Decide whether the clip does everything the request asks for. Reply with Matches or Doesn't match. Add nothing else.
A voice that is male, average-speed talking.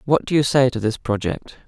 Doesn't match